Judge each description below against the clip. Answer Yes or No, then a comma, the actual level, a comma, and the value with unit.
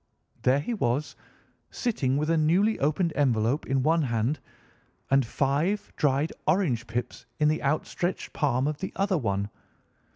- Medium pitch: Yes, medium, 145 Hz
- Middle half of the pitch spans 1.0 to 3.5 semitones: No, average, 4.4 semitones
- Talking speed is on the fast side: No, average, 150 wpm